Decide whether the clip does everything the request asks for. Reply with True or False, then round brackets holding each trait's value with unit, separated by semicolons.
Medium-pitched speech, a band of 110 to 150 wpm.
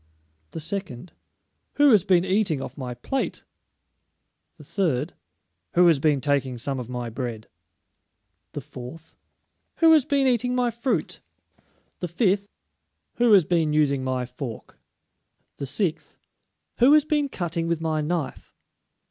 True (165 Hz; 140 wpm)